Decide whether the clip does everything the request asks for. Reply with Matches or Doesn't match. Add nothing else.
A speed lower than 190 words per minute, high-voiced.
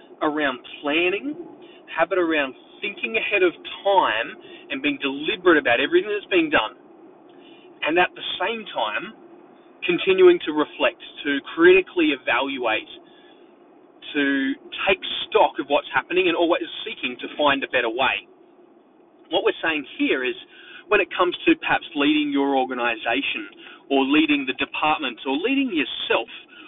Matches